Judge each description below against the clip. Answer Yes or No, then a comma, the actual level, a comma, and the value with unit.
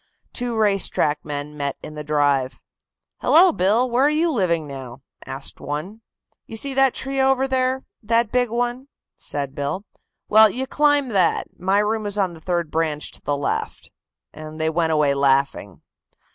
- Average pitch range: No, wide, 8.7 semitones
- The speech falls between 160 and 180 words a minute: Yes, average, 175 wpm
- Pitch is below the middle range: No, high, 190 Hz